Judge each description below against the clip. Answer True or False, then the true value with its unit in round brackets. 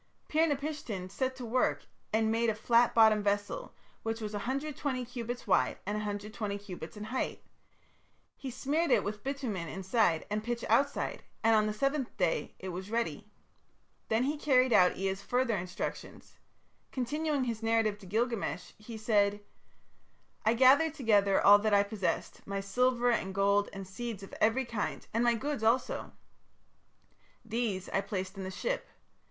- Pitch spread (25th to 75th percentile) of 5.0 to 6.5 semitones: False (3.8 semitones)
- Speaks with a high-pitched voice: True (220 Hz)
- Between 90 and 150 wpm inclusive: False (160 wpm)